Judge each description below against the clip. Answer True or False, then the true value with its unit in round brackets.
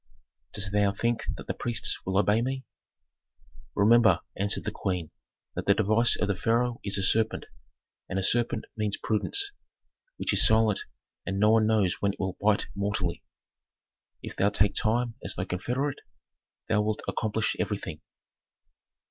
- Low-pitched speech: True (105 Hz)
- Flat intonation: True (2.3 semitones)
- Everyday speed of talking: True (160 wpm)